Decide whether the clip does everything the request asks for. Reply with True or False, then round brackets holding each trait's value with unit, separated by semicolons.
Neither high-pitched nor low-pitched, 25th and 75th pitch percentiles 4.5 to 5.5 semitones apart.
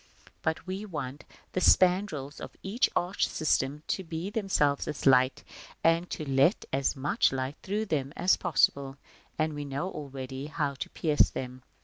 True (150 Hz; 4.8 semitones)